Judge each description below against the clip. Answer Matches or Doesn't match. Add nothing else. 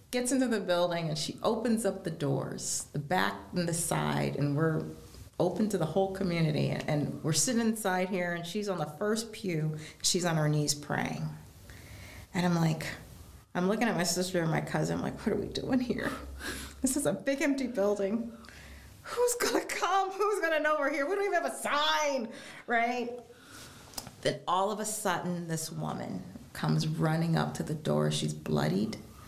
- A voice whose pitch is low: Doesn't match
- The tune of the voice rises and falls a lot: Matches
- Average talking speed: Matches